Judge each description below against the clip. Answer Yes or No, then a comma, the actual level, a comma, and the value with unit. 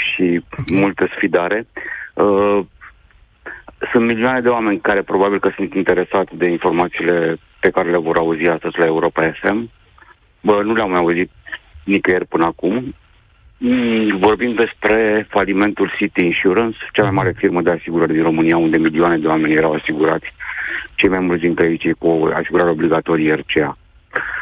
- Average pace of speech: Yes, average, 145 wpm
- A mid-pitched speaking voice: No, very low, 90 Hz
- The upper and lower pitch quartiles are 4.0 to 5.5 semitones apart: No, average, 3.6 semitones